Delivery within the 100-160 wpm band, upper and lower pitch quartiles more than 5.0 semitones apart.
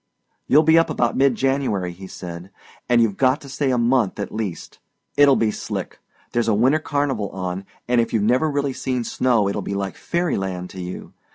No: fast, 205 wpm; wide, 5.6 semitones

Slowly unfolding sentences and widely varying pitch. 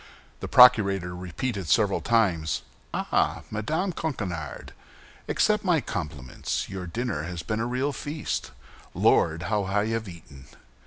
Yes: slow, 125 wpm; wide, 6.3 semitones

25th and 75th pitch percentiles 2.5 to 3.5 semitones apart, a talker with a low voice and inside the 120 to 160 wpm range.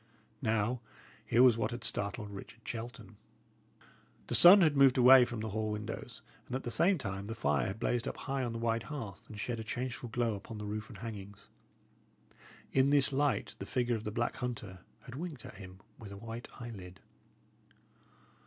No: average, 3.1 semitones; low, 115 Hz; average, 190 wpm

